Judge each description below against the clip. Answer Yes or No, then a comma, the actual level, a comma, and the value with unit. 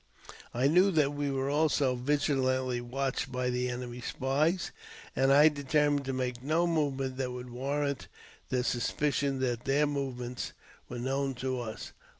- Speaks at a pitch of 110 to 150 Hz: Yes, low, 135 Hz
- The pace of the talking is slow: No, average, 150 wpm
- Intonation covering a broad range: No, narrow, 2.4 semitones